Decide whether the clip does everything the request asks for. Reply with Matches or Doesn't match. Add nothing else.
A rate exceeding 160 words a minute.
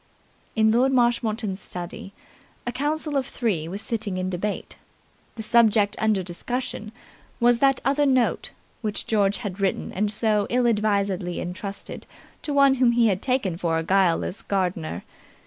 Doesn't match